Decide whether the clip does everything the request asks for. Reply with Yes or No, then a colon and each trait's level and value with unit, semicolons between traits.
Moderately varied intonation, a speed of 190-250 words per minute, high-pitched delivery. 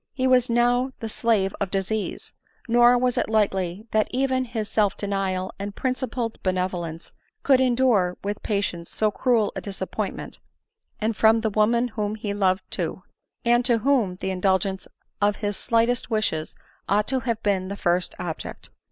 No: average, 3.8 semitones; average, 175 wpm; high, 215 Hz